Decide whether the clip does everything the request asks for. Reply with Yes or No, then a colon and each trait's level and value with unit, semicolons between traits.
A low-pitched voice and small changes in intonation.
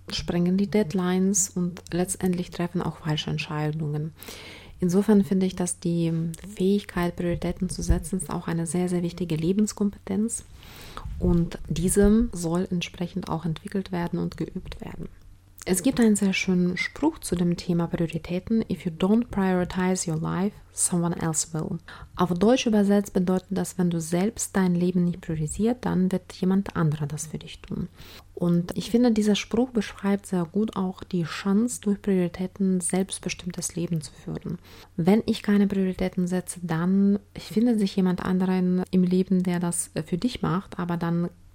No: medium, 185 Hz; narrow, 2.3 semitones